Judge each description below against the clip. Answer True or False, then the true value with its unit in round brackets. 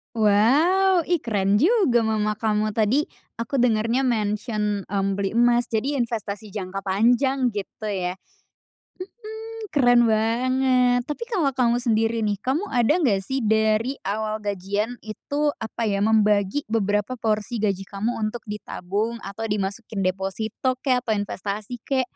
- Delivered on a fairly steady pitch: False (3.2 semitones)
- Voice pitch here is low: False (220 Hz)